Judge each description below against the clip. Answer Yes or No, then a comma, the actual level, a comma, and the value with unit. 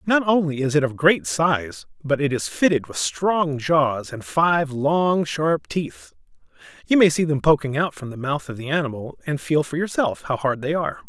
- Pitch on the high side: No, medium, 145 Hz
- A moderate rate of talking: No, fast, 210 wpm